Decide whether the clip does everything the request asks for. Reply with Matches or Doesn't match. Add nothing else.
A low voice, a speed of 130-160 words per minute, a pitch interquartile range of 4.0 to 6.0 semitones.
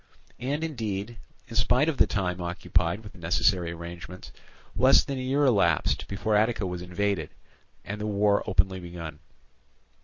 Matches